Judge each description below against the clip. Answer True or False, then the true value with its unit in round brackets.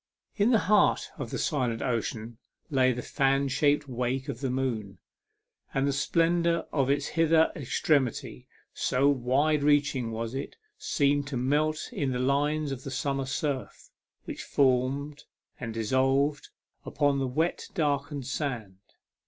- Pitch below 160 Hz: True (135 Hz)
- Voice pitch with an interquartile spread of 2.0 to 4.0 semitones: True (2.5 semitones)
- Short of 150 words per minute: True (140 wpm)